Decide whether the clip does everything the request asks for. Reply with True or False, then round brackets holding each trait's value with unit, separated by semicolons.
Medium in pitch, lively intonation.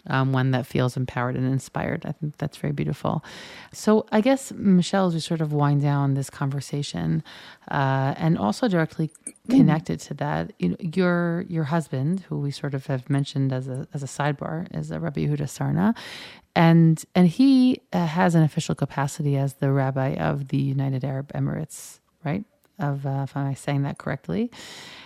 False (145 Hz; 3.7 semitones)